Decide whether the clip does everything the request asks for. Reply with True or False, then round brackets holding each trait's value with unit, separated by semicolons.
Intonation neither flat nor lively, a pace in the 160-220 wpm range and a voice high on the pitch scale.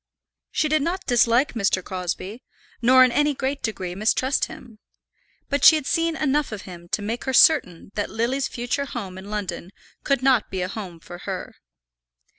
False (6.0 semitones; 180 wpm; 240 Hz)